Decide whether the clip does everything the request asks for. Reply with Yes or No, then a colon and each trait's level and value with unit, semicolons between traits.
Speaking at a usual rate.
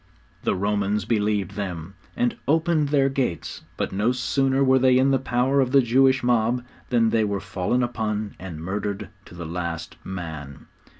Yes: average, 170 wpm